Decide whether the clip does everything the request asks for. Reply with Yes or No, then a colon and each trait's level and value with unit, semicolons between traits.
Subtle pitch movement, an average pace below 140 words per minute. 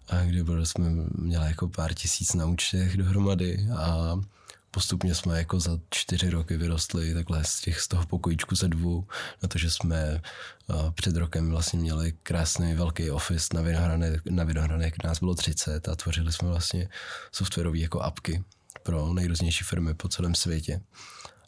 No: narrow, 1.6 semitones; average, 155 wpm